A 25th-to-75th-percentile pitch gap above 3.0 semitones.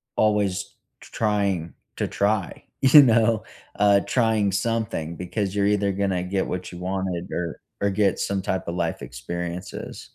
No: narrow, 2.5 semitones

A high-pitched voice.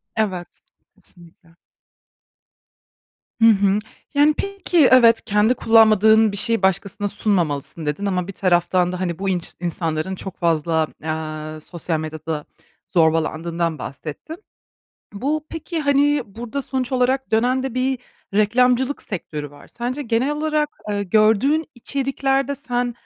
Yes: high, 210 Hz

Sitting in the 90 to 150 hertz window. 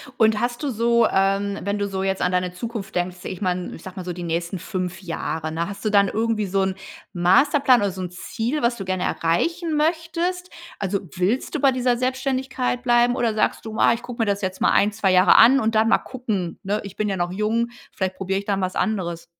No: high, 205 Hz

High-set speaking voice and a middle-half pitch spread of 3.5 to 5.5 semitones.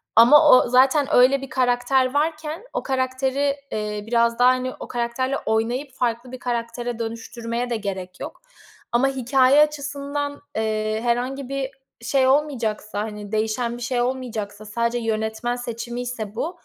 No: high, 245 Hz; average, 2.8 semitones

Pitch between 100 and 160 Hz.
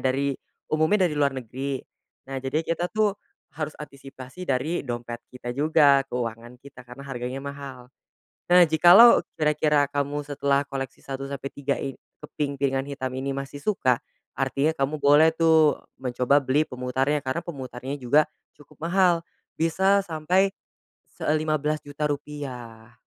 Yes: medium, 140 Hz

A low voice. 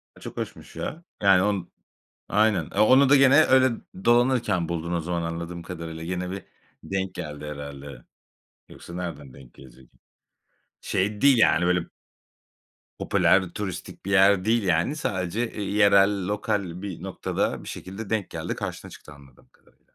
Yes: very low, 95 Hz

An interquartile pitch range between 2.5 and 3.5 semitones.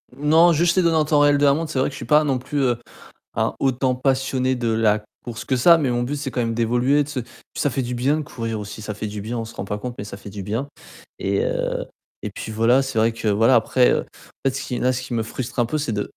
No: average, 4.1 semitones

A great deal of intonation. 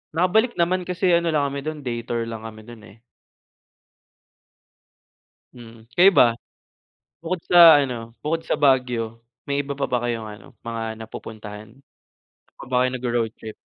Yes: wide, 6.2 semitones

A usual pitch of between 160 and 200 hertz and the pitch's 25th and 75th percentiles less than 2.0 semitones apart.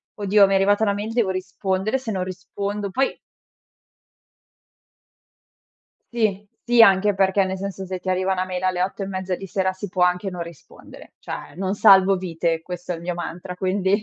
Yes: high, 190 Hz; narrow, 1.5 semitones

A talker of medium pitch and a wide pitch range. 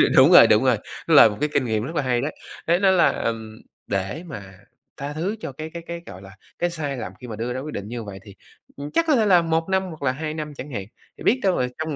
Yes: medium, 145 Hz; wide, 6.7 semitones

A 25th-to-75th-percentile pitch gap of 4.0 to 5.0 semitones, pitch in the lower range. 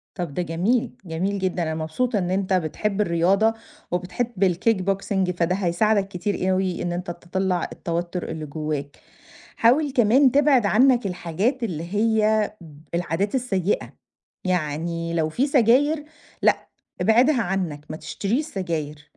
No: average, 4.6 semitones; high, 190 Hz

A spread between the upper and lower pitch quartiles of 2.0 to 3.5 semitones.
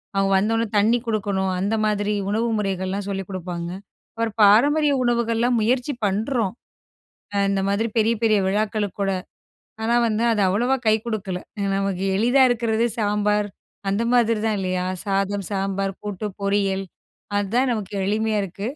Yes: narrow, 2.5 semitones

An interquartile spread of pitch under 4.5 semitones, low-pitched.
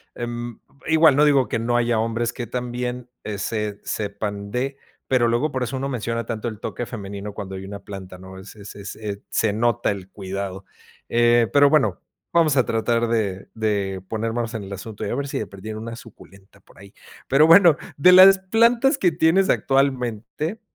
No: average, 4.8 semitones; low, 115 Hz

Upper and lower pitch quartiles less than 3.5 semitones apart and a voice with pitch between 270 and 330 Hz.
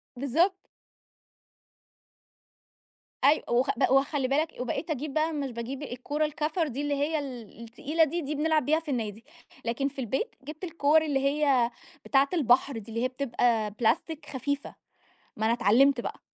No: average, 3.8 semitones; very high, 275 Hz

